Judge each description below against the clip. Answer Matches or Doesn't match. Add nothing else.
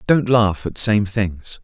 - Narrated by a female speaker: Doesn't match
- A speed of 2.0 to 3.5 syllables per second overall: Matches